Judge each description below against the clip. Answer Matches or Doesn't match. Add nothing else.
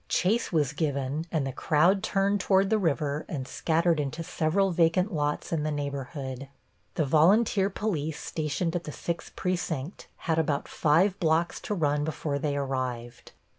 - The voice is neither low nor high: Matches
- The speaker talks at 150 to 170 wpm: Matches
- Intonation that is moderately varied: Matches